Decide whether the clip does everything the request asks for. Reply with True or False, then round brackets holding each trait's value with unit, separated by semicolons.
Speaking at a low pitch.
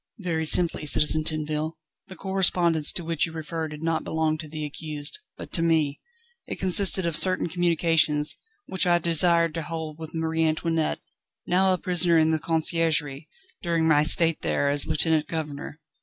False (160 Hz)